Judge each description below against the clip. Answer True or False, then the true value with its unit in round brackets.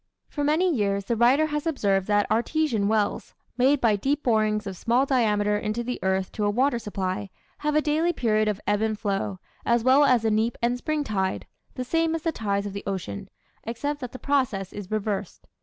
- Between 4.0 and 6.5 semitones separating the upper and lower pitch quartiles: True (5.2 semitones)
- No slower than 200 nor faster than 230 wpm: True (205 wpm)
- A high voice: True (225 Hz)